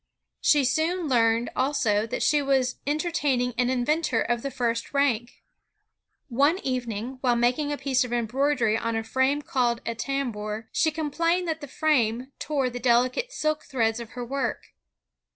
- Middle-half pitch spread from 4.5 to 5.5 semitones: No, average, 3.6 semitones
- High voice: Yes, very high, 255 Hz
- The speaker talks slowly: No, average, 160 wpm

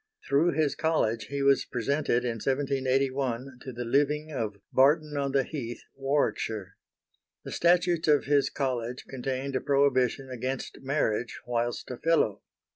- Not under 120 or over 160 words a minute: Yes, average, 140 wpm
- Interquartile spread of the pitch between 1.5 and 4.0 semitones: Yes, average, 2.7 semitones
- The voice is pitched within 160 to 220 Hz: No, low, 135 Hz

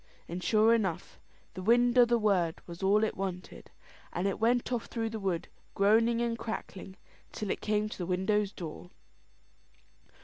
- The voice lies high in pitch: Yes, high, 210 Hz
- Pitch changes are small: No, average, 3.5 semitones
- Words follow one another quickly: No, average, 165 wpm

